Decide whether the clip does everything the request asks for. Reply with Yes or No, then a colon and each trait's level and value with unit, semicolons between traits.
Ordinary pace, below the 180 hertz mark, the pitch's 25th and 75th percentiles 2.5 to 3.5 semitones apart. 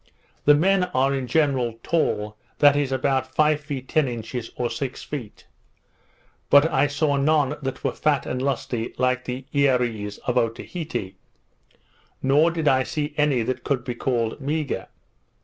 Yes: average, 155 wpm; low, 135 Hz; average, 2.9 semitones